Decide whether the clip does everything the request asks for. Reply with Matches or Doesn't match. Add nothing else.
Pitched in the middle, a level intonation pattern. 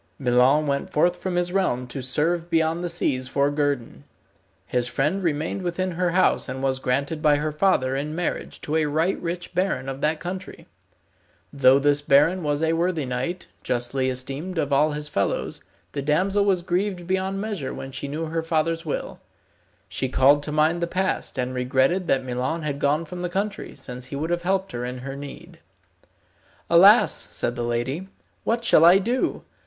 Doesn't match